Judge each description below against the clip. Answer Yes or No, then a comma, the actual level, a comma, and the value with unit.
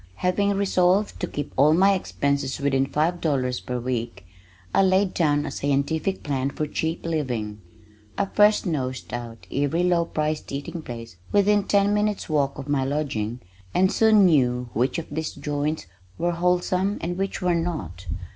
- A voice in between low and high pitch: Yes, medium, 155 Hz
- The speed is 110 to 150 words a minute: No, average, 165 wpm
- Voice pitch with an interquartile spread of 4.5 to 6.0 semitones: Yes, average, 5.2 semitones